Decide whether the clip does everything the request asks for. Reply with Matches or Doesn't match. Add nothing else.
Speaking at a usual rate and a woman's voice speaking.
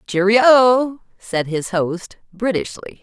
Doesn't match